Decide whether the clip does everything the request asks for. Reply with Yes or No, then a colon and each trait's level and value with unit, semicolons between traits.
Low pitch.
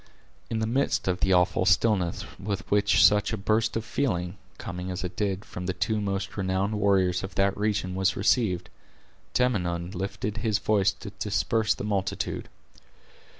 Yes: low, 100 Hz